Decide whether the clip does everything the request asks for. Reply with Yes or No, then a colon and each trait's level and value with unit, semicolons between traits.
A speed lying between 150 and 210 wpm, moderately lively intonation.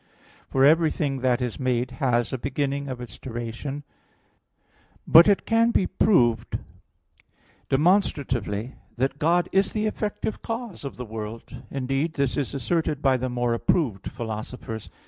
No: average, 140 wpm; average, 4.9 semitones